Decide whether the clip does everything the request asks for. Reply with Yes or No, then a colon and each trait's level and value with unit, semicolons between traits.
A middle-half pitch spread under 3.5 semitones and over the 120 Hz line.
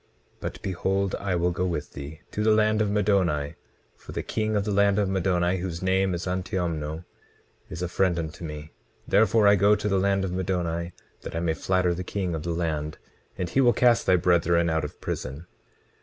No: average, 2.8 semitones; very low, 90 Hz